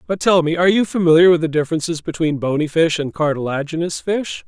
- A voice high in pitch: No, medium, 165 Hz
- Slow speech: No, average, 200 wpm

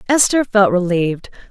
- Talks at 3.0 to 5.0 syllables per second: No, 5.2 syllables/s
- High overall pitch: Yes, high, 205 Hz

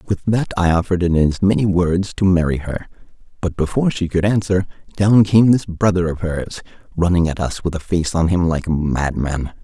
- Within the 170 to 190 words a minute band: No, fast, 205 wpm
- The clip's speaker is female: No, male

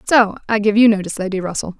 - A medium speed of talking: No, fast, 235 wpm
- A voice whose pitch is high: Yes, high, 210 Hz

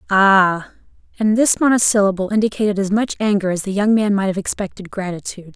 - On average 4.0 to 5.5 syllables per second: No, 6.0 syllables/s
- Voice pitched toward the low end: No, high, 200 Hz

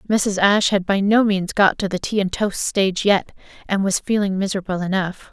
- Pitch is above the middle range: Yes, high, 195 Hz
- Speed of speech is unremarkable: No, fast, 215 wpm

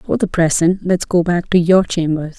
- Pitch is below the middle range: No, medium, 170 Hz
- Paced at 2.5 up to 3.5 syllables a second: No, 5.0 syllables/s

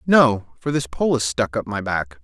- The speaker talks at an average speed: No, fast, 240 wpm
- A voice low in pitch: Yes, low, 120 Hz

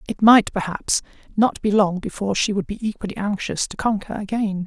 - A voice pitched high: Yes, high, 205 Hz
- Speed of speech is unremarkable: Yes, average, 195 wpm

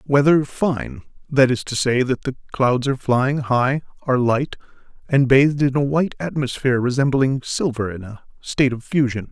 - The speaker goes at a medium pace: Yes, average, 175 wpm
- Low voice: Yes, low, 130 Hz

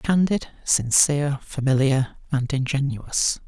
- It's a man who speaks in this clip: Yes, male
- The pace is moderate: No, slow, 85 wpm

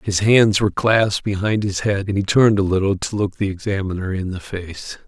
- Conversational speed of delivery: No, fast, 225 wpm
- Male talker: Yes, male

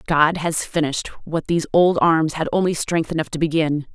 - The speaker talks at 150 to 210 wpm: Yes, average, 200 wpm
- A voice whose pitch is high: No, medium, 160 Hz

